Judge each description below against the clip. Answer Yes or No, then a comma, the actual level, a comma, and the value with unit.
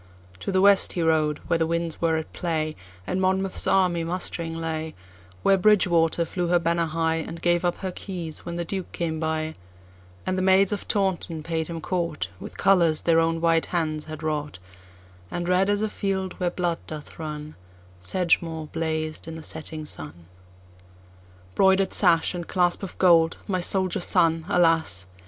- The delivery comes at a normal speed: Yes, average, 155 wpm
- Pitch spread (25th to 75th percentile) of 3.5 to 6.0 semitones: No, average, 2.9 semitones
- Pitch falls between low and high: Yes, medium, 165 Hz